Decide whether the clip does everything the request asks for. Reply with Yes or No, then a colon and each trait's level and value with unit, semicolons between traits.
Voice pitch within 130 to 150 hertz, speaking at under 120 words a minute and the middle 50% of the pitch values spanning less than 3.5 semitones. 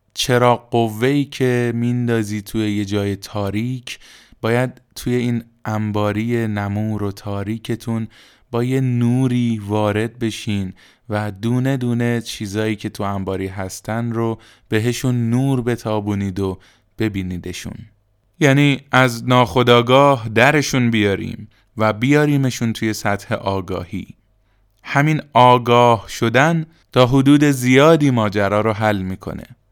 No: low, 115 Hz; average, 110 wpm; average, 3.0 semitones